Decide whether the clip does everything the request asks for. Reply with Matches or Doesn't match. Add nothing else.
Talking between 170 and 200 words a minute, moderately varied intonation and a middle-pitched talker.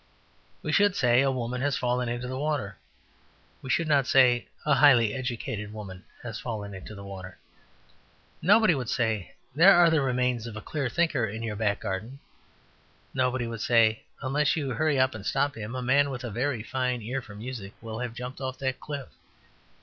Doesn't match